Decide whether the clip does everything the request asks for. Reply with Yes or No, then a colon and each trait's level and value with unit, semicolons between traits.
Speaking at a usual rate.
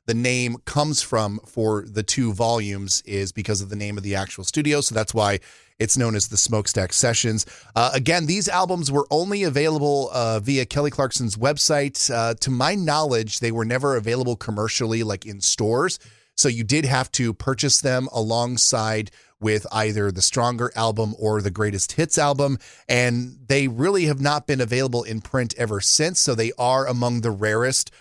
Yes: average, 180 wpm